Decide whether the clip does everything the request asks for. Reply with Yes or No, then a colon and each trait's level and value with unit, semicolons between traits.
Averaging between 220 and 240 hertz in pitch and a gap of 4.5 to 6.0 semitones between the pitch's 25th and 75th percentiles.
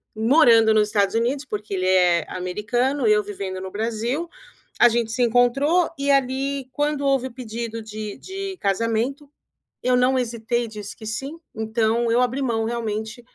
No: high, 235 Hz; average, 3.4 semitones